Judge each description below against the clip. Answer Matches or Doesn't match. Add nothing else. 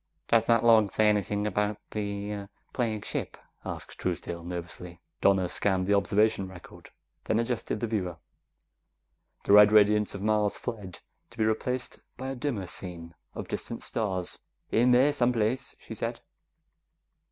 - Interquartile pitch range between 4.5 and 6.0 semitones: Doesn't match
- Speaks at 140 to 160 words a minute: Matches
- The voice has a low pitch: Matches